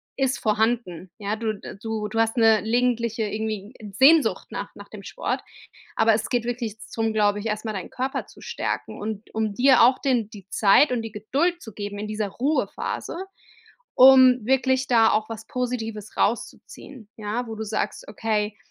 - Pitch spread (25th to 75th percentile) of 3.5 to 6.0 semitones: No, average, 2.8 semitones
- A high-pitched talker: Yes, high, 225 Hz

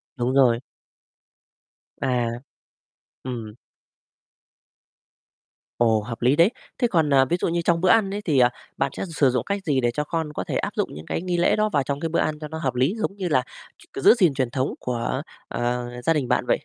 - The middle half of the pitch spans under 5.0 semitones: No, average, 5.3 semitones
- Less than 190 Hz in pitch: Yes, medium, 140 Hz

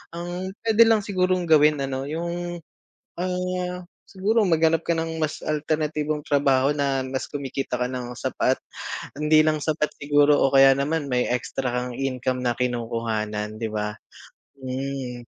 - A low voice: No, medium, 145 Hz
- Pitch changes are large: No, average, 4.4 semitones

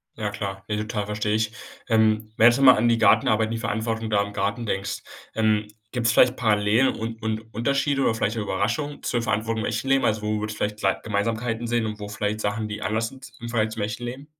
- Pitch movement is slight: Yes, narrow, 1.6 semitones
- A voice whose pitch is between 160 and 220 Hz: No, low, 110 Hz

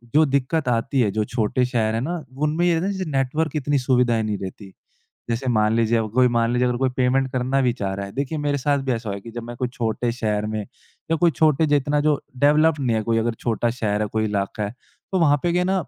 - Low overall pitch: Yes, low, 125 Hz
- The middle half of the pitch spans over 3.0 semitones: Yes, average, 4.5 semitones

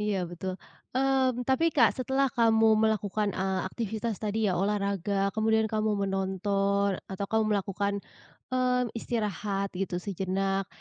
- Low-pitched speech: No, high, 205 Hz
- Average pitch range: No, narrow, 2.3 semitones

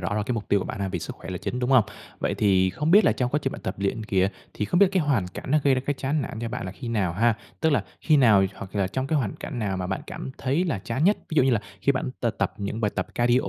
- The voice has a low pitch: Yes, low, 120 Hz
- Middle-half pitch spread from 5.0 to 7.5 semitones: Yes, wide, 5.6 semitones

